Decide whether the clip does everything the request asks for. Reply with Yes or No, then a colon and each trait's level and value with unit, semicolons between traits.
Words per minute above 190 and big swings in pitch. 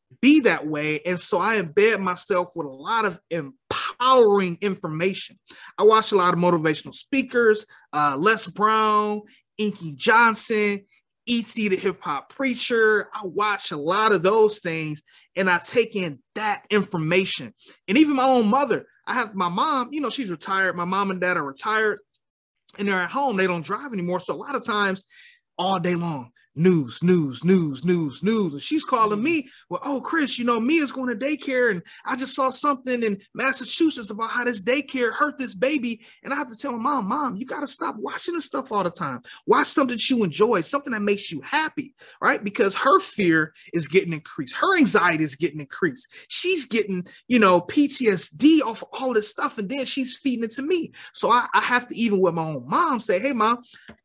Yes: average, 200 wpm; wide, 6.3 semitones